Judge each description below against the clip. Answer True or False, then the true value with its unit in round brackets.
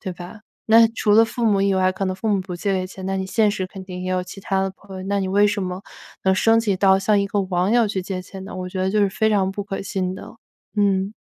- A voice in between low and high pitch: False (195 Hz)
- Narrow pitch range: True (1.6 semitones)